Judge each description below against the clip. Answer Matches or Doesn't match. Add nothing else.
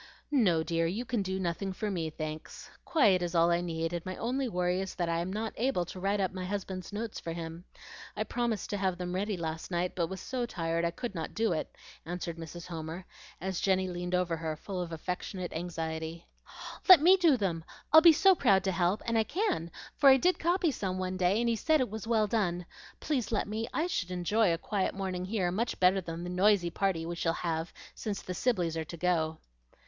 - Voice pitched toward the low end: Doesn't match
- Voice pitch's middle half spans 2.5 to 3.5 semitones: Doesn't match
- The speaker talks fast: Matches